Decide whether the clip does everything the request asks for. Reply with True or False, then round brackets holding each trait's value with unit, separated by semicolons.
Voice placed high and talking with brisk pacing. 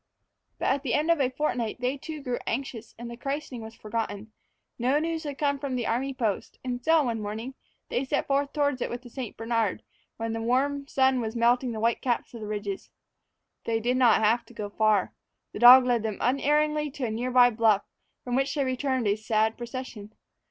True (245 Hz; 215 wpm)